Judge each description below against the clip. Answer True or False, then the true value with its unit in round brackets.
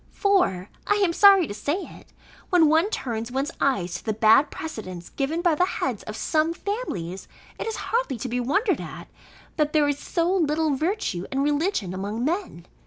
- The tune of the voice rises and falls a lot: True (8.2 semitones)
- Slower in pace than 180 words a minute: False (185 wpm)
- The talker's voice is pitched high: True (295 Hz)